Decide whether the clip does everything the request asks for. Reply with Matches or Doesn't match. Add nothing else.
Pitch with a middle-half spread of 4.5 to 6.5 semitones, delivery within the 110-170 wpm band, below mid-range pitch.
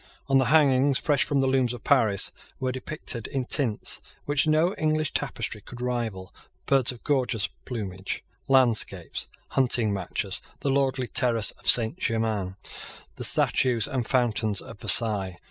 Doesn't match